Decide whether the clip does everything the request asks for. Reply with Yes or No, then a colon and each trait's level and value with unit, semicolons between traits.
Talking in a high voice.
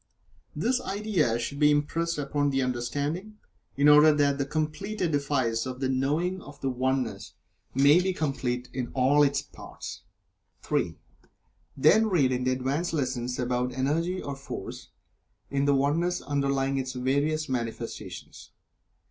No: medium, 140 Hz